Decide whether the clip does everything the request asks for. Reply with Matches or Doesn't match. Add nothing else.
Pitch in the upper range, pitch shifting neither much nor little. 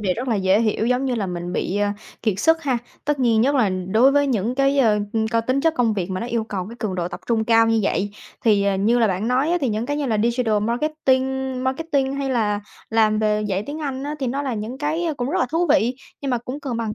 Matches